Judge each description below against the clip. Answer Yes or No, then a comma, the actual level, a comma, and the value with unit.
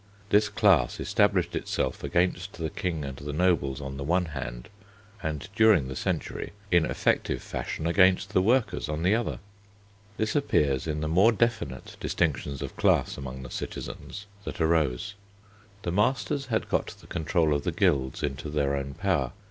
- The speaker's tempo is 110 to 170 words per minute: Yes, average, 165 wpm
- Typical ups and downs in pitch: No, wide, 5.9 semitones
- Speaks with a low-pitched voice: Yes, very low, 80 Hz